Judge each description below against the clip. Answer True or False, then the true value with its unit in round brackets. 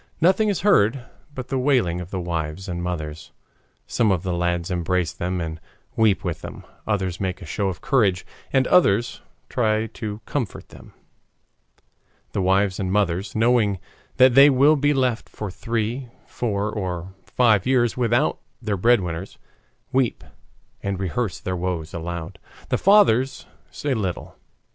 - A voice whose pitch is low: True (100 Hz)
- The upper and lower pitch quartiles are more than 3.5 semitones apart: True (5.4 semitones)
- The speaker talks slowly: False (150 wpm)